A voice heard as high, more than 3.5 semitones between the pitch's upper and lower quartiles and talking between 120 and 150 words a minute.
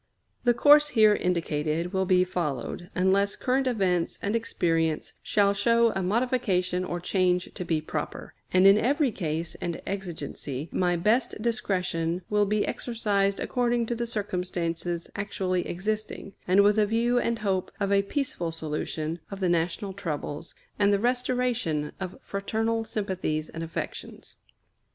Yes: high, 195 Hz; average, 4.1 semitones; average, 145 wpm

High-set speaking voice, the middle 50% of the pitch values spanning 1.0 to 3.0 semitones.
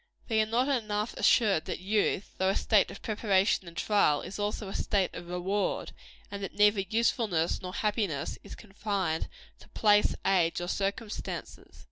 Yes: high, 200 Hz; narrow, 2.5 semitones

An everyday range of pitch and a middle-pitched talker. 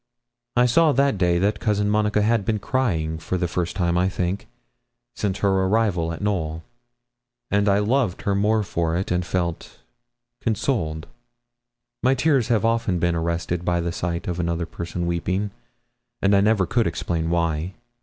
No: average, 3.7 semitones; very low, 95 Hz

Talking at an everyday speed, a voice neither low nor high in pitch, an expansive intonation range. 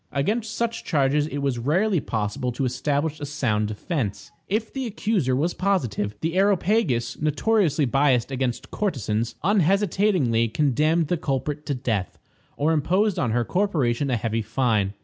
Yes: average, 150 wpm; medium, 145 Hz; wide, 7.3 semitones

